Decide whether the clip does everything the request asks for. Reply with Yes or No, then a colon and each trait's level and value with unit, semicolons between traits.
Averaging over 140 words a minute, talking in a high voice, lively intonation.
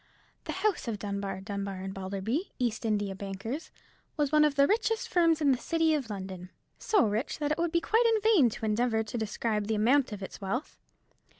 Yes: average, 200 wpm; high, 230 Hz; wide, 7.4 semitones